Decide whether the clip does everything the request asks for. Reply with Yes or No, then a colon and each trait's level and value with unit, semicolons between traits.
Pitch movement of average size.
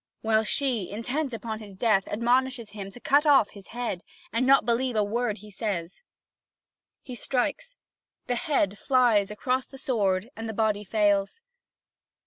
Yes: average, 3.6 semitones